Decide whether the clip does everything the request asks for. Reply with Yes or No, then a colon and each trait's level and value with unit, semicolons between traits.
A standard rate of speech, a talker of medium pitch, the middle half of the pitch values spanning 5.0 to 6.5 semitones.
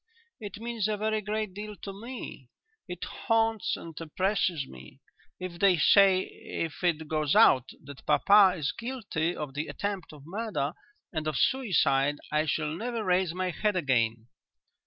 Yes: average, 155 wpm; medium, 180 Hz; wide, 5.6 semitones